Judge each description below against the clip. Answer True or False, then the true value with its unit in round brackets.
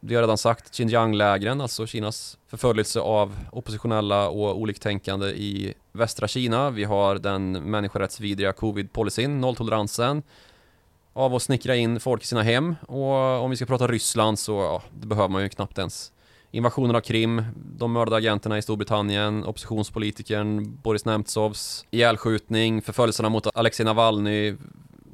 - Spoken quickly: False (140 wpm)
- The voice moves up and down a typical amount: False (2.1 semitones)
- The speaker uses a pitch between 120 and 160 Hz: False (110 Hz)